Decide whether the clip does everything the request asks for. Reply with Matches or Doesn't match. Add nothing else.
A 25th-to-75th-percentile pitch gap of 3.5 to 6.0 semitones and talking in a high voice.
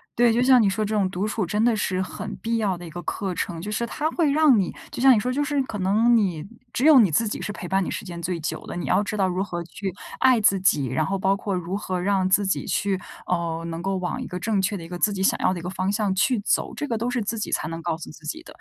Matches